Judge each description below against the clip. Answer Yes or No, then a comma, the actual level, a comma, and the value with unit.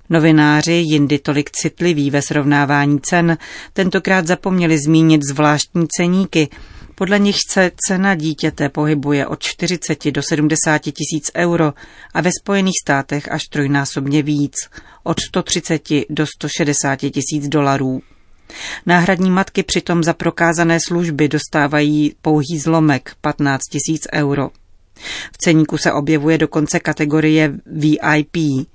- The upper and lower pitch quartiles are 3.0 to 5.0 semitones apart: No, narrow, 2.5 semitones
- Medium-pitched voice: Yes, medium, 155 Hz